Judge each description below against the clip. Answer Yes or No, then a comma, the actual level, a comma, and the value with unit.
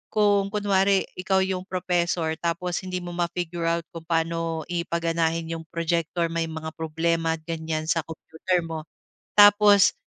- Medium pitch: Yes, medium, 170 Hz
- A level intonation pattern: Yes, narrow, 2.0 semitones